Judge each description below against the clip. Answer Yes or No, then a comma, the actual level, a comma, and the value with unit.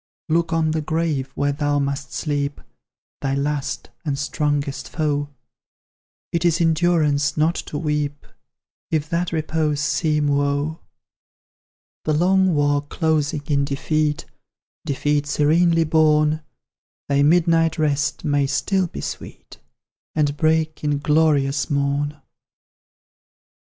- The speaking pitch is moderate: Yes, medium, 150 Hz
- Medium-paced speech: No, slow, 115 wpm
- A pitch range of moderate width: No, narrow, 1.9 semitones